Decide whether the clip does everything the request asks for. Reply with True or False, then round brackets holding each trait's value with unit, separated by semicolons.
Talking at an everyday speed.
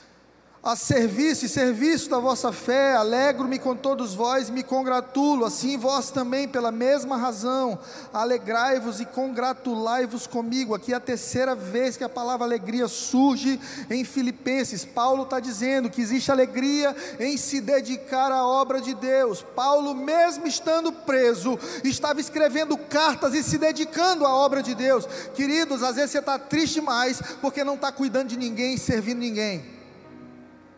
True (155 wpm)